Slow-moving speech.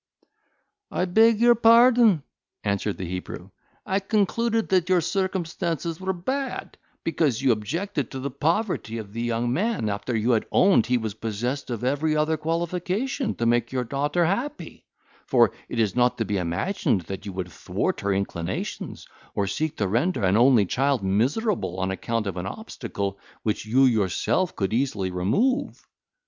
No: average, 165 wpm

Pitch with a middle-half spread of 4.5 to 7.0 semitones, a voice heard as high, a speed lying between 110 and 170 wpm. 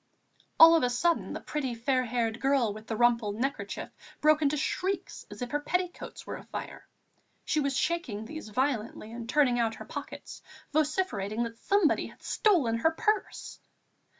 Yes: average, 5.2 semitones; very high, 265 Hz; average, 165 wpm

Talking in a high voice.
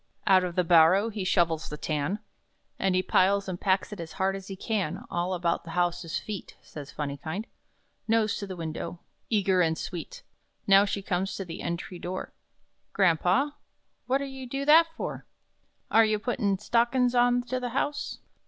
Yes: high, 195 Hz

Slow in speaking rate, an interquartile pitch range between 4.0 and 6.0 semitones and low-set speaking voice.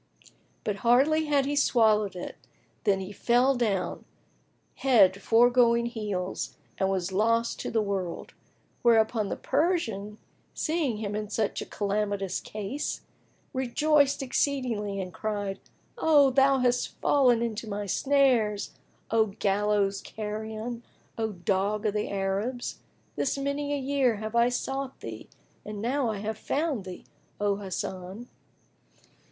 No: slow, 125 wpm; average, 4.3 semitones; high, 220 Hz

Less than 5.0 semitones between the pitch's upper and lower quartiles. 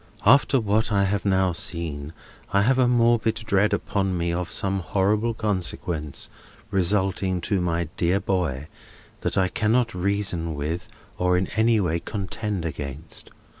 Yes: average, 3.5 semitones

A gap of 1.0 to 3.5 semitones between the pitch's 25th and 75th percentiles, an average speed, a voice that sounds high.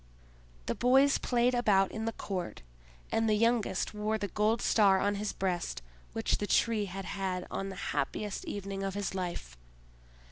Yes: narrow, 2.5 semitones; average, 170 wpm; high, 205 Hz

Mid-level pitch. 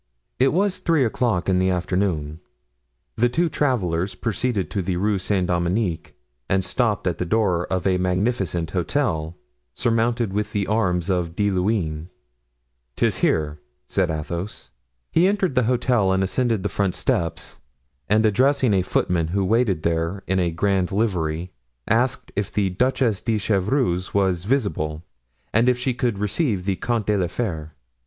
No: low, 100 Hz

